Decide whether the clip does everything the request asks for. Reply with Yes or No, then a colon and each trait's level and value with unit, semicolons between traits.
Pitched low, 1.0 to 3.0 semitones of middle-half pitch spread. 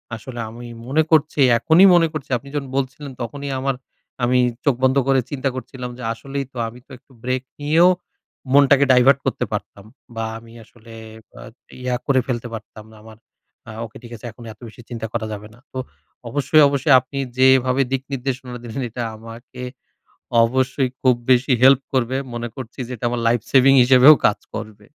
Yes: low, 130 Hz; narrow, 2.6 semitones